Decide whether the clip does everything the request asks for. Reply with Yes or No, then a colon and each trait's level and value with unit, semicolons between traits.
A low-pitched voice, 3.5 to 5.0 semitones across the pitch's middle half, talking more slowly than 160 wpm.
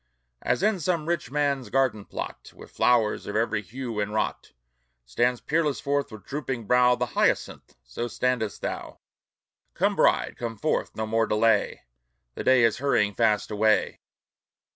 Yes: low, 120 Hz; average, 3.9 semitones; average, 150 wpm